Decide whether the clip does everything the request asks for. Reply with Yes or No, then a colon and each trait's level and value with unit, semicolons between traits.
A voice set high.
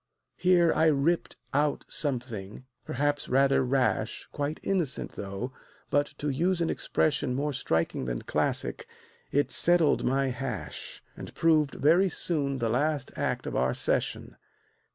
No: medium, 140 Hz